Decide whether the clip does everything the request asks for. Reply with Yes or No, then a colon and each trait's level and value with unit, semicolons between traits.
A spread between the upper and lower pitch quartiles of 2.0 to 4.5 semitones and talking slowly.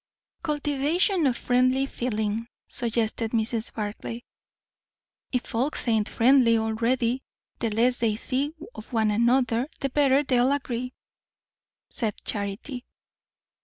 Yes: average, 3.0 semitones; slow, 110 wpm